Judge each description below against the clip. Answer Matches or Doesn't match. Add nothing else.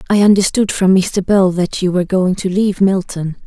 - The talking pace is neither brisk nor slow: Doesn't match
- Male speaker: Doesn't match